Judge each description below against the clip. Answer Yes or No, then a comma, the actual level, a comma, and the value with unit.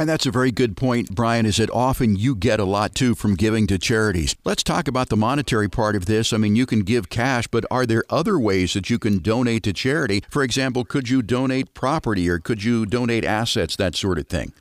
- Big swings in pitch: No, average, 3.1 semitones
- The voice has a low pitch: Yes, low, 115 Hz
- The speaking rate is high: Yes, fast, 240 wpm